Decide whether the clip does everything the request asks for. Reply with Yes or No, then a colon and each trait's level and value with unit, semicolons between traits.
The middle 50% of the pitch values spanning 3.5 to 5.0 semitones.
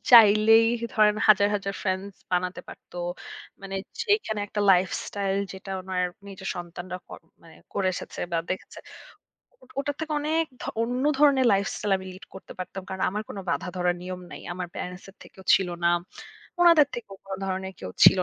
No: average, 2.7 semitones